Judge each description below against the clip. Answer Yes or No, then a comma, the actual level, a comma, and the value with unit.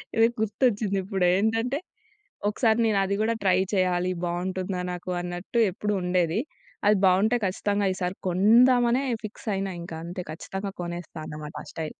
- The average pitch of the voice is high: Yes, high, 195 Hz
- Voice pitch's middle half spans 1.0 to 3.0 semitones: No, average, 3.5 semitones